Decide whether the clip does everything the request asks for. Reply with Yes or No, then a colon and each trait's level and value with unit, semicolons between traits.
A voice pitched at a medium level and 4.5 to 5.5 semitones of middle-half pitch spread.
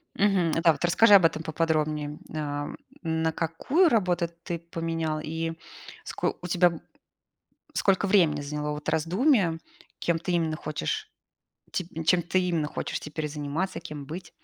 No: medium, 165 Hz; average, 2.7 semitones